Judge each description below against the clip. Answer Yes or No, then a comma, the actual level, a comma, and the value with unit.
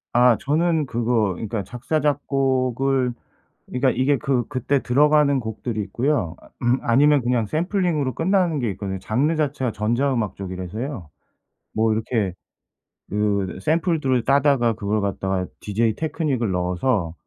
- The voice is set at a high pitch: No, low, 125 Hz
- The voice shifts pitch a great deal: No, average, 4.9 semitones